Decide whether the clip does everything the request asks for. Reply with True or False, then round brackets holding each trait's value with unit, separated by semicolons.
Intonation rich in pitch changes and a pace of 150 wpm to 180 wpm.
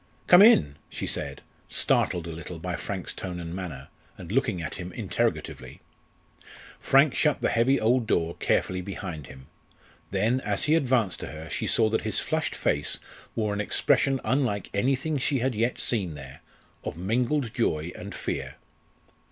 True (6.8 semitones; 165 wpm)